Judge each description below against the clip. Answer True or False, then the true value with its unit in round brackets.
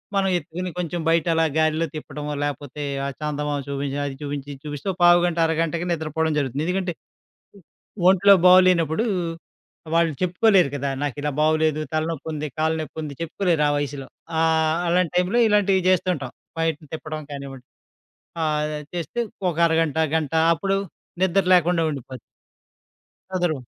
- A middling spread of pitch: True (3.0 semitones)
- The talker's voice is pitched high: False (160 Hz)